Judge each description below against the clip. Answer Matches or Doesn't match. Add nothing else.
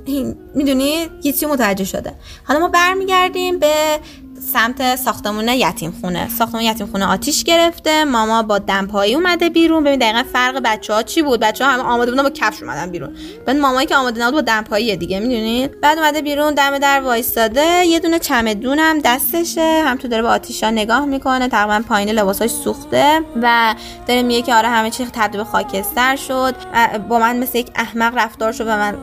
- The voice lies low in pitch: Doesn't match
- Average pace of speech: Doesn't match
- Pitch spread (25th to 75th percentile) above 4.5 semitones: Matches